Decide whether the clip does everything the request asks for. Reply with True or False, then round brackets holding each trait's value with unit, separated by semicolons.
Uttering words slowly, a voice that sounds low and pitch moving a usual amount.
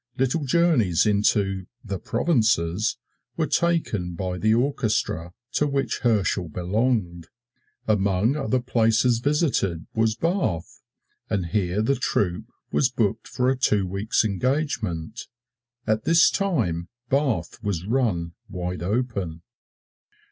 False (115 wpm; 110 Hz; 6.1 semitones)